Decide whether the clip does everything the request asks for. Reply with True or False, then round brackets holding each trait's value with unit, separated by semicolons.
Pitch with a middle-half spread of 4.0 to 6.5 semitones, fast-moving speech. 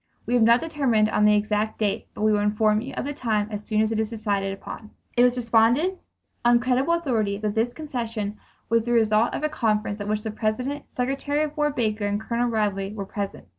False (2.8 semitones; 225 wpm)